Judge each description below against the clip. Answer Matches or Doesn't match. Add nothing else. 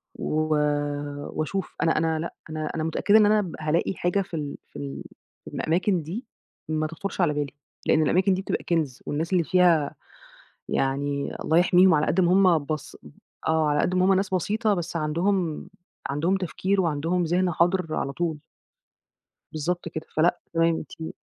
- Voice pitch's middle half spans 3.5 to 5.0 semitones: Doesn't match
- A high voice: Doesn't match